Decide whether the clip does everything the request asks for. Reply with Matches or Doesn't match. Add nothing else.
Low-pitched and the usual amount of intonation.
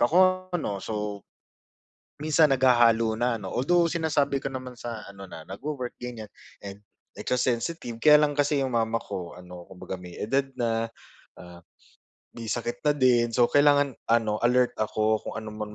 Matches